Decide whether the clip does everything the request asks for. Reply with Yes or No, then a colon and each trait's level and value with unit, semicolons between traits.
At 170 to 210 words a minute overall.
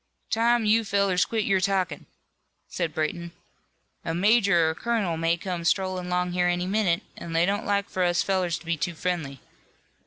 Yes: average, 185 wpm